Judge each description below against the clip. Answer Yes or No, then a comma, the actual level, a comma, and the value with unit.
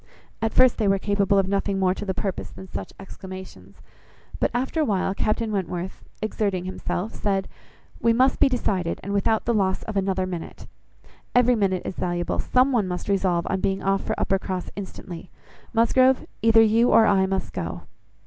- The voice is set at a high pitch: Yes, high, 195 Hz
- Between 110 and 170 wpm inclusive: No, average, 180 wpm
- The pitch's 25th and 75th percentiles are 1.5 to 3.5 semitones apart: Yes, average, 3.0 semitones